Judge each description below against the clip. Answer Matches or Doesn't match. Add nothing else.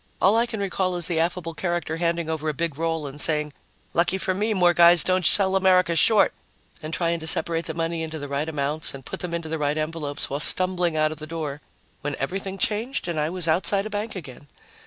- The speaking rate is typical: Doesn't match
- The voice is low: Doesn't match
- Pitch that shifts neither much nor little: Matches